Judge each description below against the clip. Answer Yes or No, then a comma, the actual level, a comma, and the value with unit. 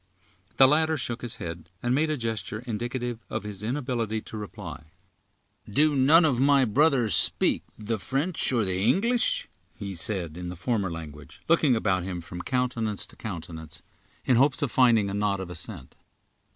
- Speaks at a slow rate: No, average, 170 wpm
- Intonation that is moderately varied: No, wide, 6.0 semitones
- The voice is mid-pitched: No, low, 110 Hz